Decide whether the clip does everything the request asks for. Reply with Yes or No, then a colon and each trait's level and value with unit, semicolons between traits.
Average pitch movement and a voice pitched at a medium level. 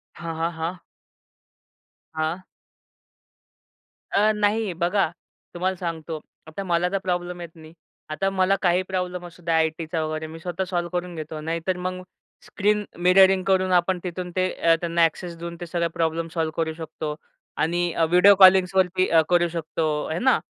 No: narrow, 2.2 semitones; medium, 175 Hz